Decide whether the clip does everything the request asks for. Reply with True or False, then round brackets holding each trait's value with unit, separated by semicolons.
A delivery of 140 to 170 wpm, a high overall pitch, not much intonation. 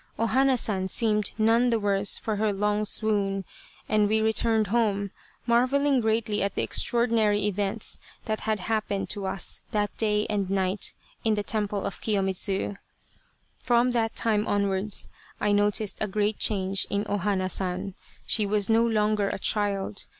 True (165 wpm; 210 Hz; 1.9 semitones)